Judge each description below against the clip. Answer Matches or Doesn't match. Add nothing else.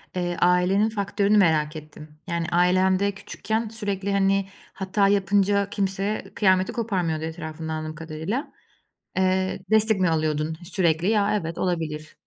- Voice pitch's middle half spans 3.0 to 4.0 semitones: Matches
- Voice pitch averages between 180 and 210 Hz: Matches